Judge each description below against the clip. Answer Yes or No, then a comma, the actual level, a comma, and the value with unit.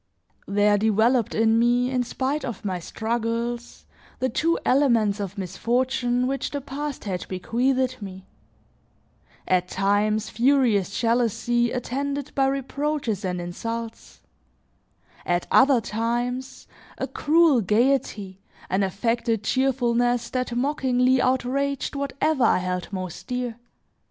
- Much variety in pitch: No, average, 3.9 semitones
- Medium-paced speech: No, slow, 115 wpm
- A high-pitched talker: Yes, high, 240 Hz